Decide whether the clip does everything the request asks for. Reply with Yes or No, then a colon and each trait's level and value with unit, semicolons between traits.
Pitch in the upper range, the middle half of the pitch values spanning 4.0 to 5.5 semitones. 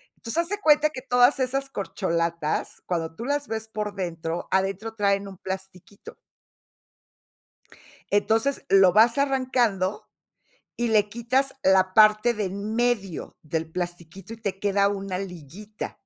Yes: high, 205 Hz; average, 4.3 semitones